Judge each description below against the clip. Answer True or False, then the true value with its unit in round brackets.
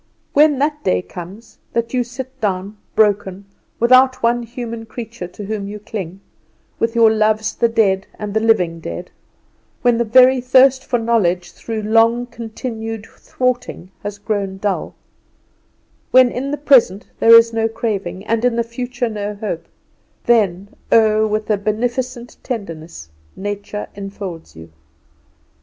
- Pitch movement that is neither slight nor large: True (3.1 semitones)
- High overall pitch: True (220 Hz)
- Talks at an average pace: True (145 wpm)